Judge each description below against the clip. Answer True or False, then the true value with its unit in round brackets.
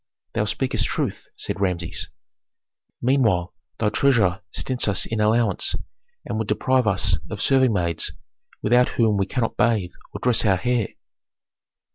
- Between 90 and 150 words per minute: True (140 wpm)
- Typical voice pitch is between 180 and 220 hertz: False (110 Hz)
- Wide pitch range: False (4.0 semitones)